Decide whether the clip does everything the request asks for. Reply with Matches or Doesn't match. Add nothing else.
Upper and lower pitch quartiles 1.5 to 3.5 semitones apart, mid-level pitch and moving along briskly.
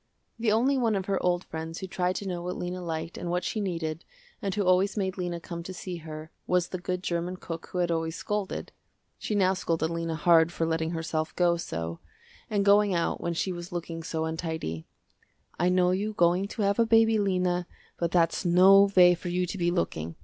Matches